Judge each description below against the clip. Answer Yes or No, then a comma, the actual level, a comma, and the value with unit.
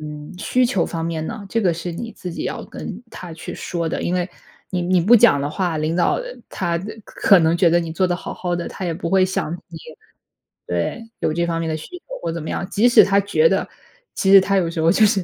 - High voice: No, medium, 175 Hz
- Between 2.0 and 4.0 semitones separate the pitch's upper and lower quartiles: Yes, average, 2.9 semitones